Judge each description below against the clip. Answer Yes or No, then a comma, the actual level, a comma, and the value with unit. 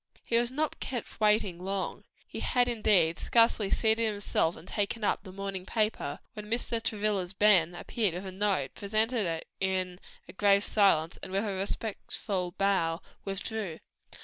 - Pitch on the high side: Yes, high, 200 Hz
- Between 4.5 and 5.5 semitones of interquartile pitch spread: No, average, 2.8 semitones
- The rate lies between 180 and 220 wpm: No, average, 150 wpm